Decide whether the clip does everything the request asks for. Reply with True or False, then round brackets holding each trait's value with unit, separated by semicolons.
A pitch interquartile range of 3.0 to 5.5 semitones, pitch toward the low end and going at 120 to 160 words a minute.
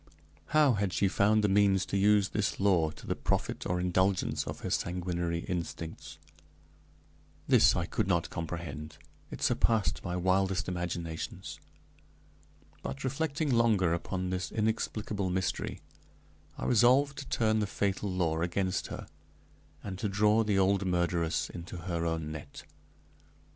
True (3.3 semitones; 95 Hz; 140 wpm)